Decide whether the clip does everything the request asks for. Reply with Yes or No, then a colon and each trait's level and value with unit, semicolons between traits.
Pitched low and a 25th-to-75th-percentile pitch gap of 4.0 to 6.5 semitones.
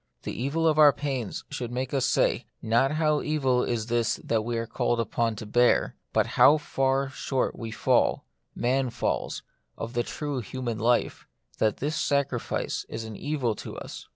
No: low, 125 Hz; average, 3.3 semitones